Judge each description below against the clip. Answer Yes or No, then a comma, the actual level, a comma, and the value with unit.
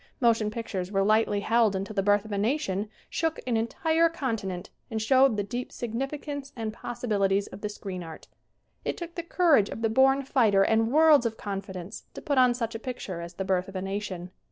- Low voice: No, high, 220 Hz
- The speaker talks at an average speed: No, fast, 210 wpm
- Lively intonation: No, average, 4.7 semitones